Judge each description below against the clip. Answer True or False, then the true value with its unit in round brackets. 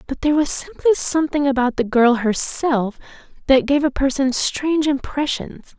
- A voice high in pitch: True (275 Hz)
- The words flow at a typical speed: True (155 wpm)